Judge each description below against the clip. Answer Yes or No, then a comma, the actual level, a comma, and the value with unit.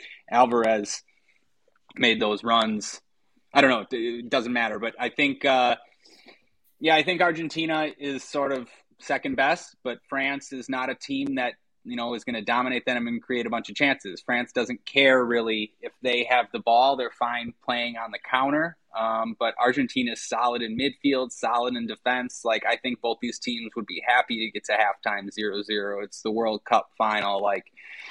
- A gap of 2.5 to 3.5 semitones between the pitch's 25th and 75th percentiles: Yes, average, 2.9 semitones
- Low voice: Yes, low, 120 Hz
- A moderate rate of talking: Yes, average, 190 wpm